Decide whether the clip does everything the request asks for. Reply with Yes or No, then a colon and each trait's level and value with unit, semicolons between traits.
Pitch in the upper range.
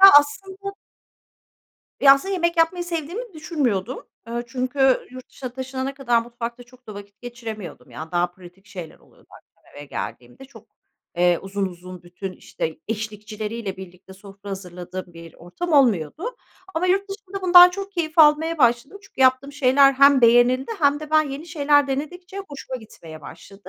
Yes: very high, 255 Hz